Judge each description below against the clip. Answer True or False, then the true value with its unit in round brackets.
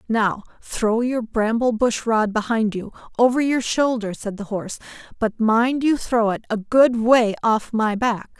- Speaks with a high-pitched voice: True (225 Hz)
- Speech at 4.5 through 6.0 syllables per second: False (4.2 syllables/s)